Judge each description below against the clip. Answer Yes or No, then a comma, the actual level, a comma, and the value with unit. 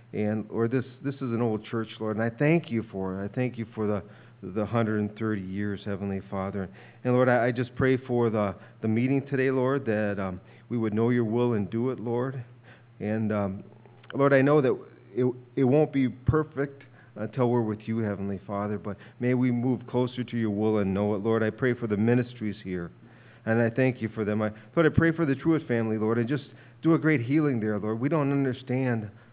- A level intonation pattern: No, average, 3.0 semitones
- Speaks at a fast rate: Yes, fast, 225 wpm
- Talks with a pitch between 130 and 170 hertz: No, low, 115 Hz